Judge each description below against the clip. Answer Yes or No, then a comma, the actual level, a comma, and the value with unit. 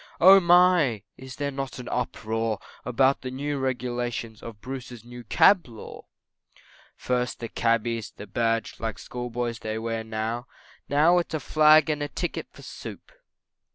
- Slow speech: No, average, 155 wpm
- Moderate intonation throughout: Yes, average, 3.8 semitones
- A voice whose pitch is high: No, low, 125 Hz